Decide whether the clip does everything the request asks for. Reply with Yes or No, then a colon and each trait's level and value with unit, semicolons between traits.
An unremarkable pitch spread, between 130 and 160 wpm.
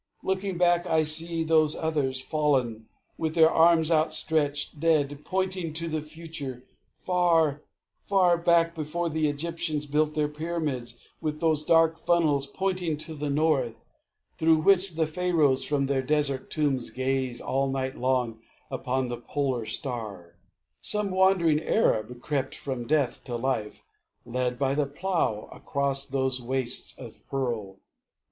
Yes: average, 3.7 semitones; average, 140 wpm